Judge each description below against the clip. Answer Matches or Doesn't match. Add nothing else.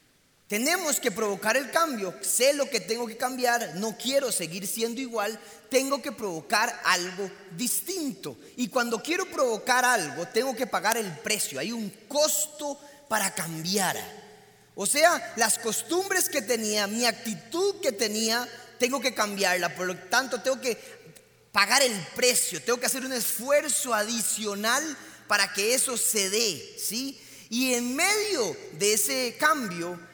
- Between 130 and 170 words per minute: Matches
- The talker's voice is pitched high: Matches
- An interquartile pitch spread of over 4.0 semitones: Matches